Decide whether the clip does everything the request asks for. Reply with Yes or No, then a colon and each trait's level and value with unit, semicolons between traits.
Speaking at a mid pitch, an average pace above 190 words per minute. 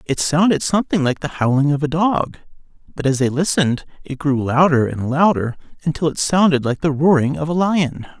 Yes: medium, 150 Hz; average, 200 wpm